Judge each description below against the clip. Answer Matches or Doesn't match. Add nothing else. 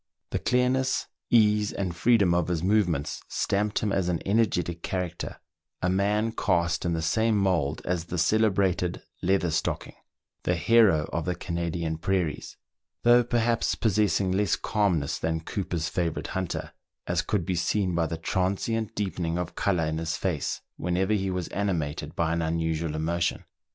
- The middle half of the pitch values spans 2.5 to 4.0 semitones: Matches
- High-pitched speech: Doesn't match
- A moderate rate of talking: Matches